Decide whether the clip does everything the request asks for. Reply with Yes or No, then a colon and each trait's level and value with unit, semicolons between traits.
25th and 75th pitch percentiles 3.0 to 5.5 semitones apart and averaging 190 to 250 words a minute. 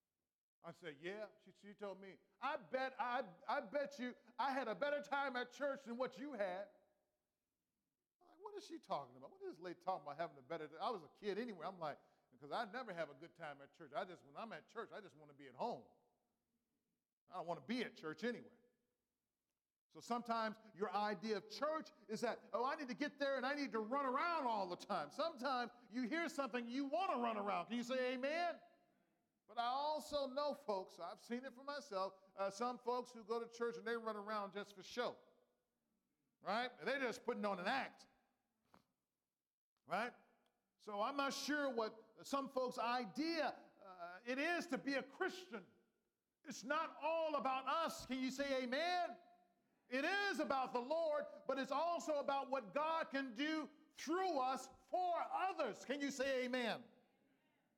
Yes: average, 5.0 semitones; average, 200 wpm